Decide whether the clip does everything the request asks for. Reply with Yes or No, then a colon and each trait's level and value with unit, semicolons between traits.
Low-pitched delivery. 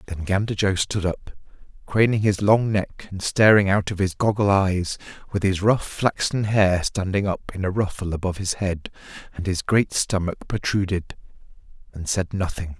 Yes: very low, 95 Hz